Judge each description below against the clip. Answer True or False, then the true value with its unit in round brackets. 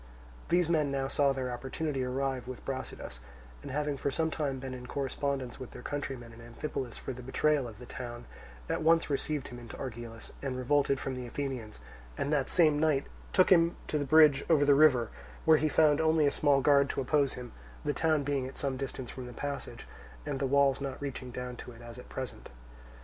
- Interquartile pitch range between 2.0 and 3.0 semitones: True (2.5 semitones)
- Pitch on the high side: False (135 Hz)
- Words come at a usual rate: False (215 wpm)